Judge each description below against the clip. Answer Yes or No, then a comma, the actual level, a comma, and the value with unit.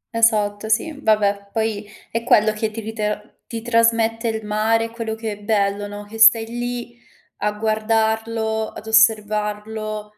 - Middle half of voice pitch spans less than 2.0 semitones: Yes, narrow, 1.3 semitones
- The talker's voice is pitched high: Yes, high, 220 Hz